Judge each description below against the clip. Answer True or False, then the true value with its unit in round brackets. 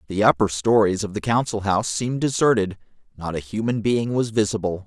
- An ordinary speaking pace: True (185 wpm)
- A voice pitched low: True (105 Hz)